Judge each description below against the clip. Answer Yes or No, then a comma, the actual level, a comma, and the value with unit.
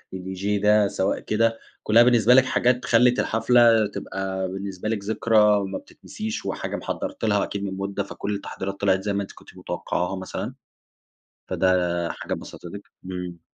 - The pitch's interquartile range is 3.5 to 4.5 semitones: No, average, 2.8 semitones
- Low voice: Yes, low, 100 Hz